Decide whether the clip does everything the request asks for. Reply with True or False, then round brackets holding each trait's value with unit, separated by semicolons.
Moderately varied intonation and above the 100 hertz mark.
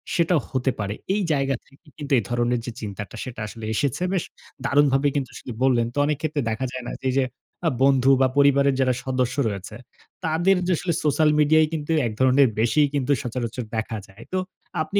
True (3.4 semitones; 135 Hz)